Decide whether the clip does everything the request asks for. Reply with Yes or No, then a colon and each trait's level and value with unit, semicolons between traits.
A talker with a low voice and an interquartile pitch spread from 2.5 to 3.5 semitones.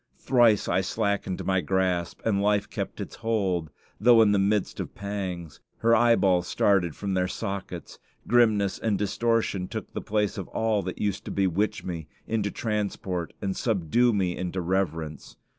Yes: low, 100 Hz; average, 2.8 semitones